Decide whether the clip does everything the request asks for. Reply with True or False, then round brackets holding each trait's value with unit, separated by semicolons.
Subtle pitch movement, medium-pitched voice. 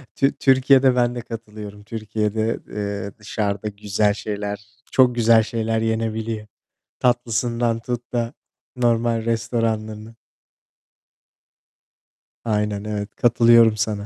False (1.9 semitones; 110 Hz)